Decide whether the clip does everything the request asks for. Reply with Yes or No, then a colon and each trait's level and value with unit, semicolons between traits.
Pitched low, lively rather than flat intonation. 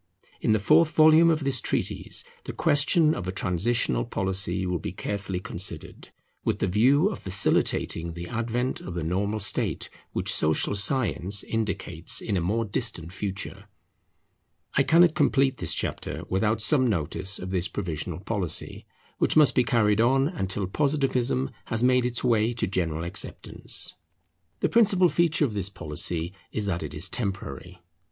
Yes: low, 100 Hz; wide, 6.1 semitones